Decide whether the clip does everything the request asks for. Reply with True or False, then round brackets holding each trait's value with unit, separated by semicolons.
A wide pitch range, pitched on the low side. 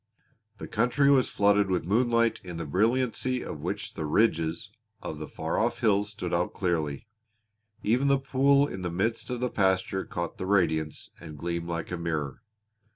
True (5.7 semitones; 95 Hz)